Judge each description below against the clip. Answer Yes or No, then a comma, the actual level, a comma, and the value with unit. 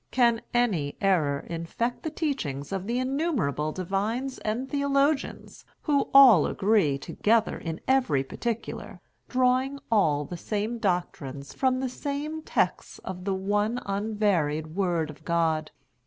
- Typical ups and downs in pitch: No, wide, 7.7 semitones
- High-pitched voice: Yes, high, 205 Hz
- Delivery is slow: Yes, slow, 130 wpm